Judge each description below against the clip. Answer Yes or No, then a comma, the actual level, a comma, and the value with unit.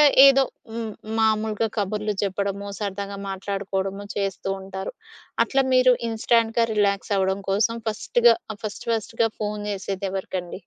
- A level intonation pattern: Yes, narrow, 2.3 semitones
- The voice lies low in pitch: No, high, 205 Hz